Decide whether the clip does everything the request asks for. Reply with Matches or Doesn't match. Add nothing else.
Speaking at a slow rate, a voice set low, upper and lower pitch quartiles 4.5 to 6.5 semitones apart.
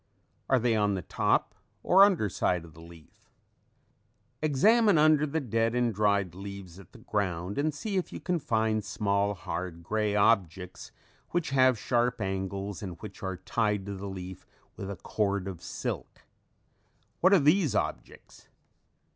Doesn't match